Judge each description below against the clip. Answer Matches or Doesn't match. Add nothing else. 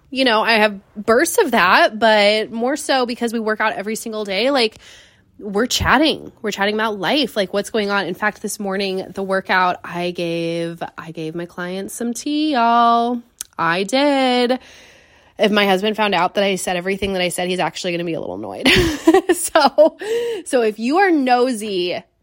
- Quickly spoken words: Doesn't match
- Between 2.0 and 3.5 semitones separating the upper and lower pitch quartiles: Doesn't match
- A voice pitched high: Matches